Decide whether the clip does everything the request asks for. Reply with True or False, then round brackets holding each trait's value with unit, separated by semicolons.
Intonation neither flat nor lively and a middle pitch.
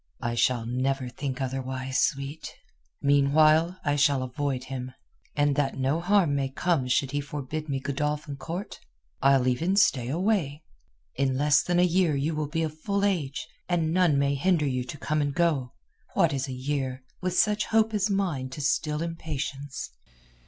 True (3.6 semitones; 145 Hz)